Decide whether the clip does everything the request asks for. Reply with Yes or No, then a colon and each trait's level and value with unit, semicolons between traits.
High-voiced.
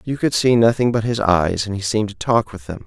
No: low, 105 Hz